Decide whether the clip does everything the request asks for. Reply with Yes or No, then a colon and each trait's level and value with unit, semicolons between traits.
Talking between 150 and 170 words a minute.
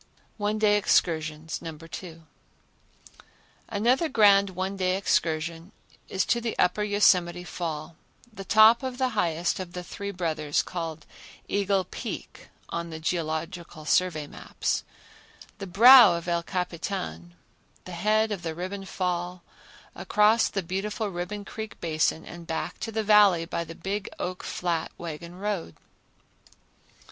No: slow, 135 wpm